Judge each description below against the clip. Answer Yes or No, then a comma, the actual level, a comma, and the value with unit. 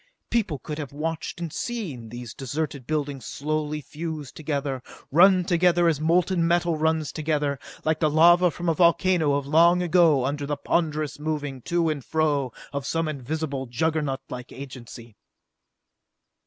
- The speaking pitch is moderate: Yes, medium, 155 Hz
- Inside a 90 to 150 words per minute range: Yes, average, 145 wpm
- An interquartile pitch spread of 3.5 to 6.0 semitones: No, average, 3.0 semitones